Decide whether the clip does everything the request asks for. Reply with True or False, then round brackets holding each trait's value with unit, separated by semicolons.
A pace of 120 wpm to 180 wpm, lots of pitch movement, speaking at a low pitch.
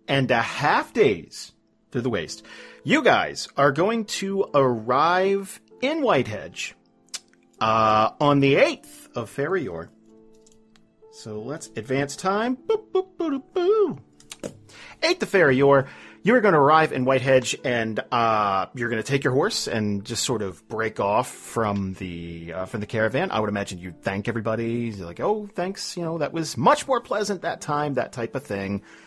True (175 wpm; 8.8 semitones; 125 Hz)